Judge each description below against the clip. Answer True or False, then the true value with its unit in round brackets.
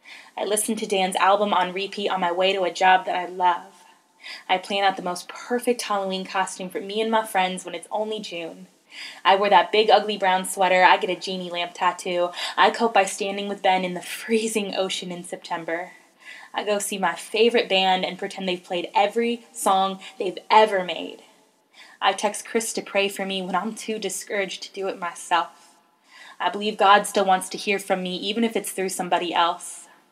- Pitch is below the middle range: False (190 Hz)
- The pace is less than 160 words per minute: False (205 wpm)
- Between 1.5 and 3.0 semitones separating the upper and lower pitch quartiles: True (2.5 semitones)